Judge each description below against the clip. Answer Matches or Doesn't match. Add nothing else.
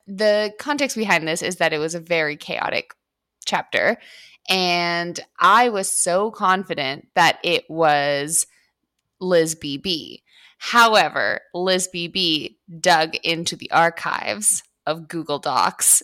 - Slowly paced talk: Matches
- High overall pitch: Doesn't match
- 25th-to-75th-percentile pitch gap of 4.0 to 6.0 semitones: Doesn't match